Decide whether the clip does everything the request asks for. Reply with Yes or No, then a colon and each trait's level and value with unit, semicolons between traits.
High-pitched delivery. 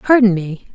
Yes: high, 205 Hz